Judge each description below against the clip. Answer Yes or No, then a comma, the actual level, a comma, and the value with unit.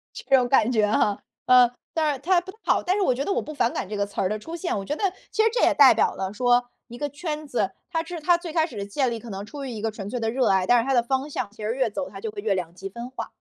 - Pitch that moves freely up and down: Yes, wide, 6.4 semitones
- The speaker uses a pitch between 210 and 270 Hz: Yes, very high, 250 Hz